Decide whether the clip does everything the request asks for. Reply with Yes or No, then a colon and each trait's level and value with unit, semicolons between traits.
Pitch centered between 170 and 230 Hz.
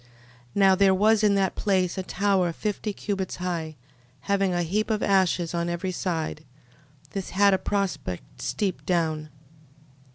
Yes: high, 190 Hz